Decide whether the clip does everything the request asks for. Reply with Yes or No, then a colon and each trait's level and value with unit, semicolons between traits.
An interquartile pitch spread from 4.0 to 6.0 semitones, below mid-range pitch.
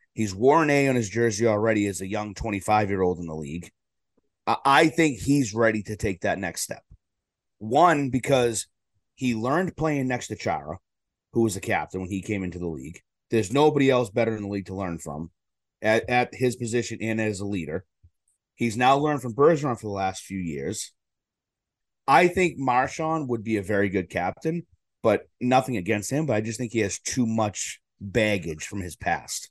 Yes: average, 4.4 semitones; low, 110 Hz